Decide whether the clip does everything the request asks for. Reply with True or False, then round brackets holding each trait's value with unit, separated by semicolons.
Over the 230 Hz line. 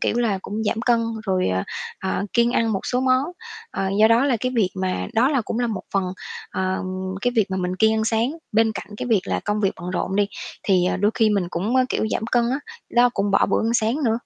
False (220 Hz)